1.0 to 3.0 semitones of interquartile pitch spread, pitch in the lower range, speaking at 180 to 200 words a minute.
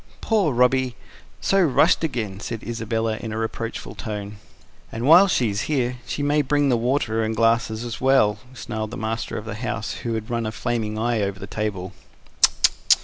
Yes: narrow, 2.6 semitones; low, 115 Hz; average, 185 wpm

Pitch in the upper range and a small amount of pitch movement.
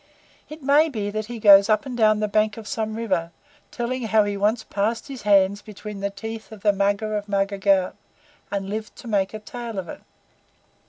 Yes: high, 215 Hz; narrow, 2.0 semitones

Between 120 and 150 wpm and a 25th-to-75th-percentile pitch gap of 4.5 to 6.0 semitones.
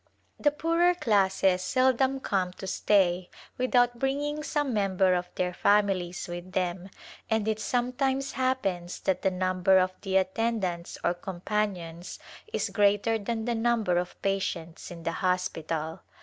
Yes: average, 145 wpm; average, 4.8 semitones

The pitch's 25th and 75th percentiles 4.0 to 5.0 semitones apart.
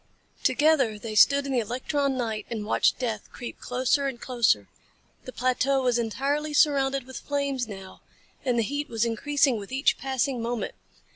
No: average, 3.3 semitones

